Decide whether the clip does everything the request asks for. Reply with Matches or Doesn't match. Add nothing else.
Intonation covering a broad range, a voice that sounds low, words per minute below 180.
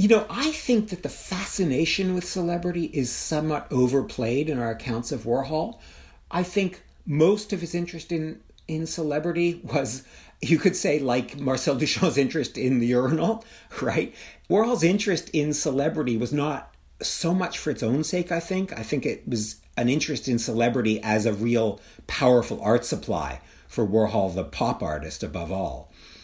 Doesn't match